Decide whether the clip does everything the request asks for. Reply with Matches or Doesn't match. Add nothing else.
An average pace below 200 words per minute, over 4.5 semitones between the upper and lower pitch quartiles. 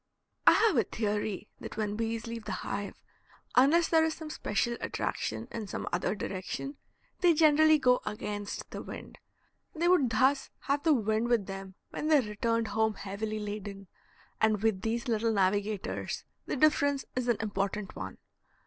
Matches